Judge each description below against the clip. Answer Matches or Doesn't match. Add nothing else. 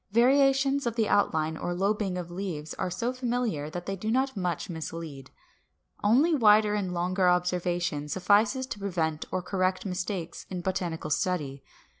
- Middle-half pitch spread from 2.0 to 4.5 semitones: Matches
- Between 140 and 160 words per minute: Matches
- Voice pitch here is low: Doesn't match